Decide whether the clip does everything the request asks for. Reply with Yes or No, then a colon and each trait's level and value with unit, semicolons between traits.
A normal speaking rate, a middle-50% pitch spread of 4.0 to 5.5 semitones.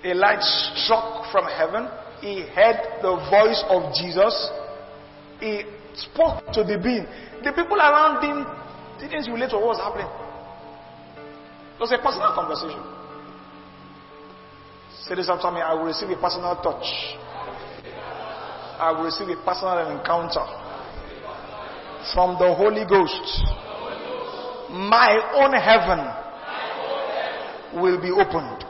No: slow, 120 wpm; average, 4.7 semitones